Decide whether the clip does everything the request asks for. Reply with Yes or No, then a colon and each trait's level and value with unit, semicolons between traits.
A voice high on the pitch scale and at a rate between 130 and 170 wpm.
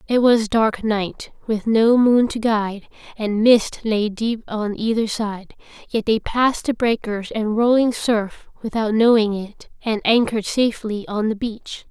Yes: high, 220 Hz; average, 165 wpm